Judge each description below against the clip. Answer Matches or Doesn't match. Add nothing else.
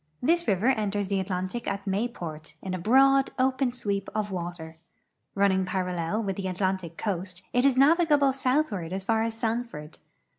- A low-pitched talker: Doesn't match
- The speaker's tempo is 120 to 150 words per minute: Doesn't match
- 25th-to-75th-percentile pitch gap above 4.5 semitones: Matches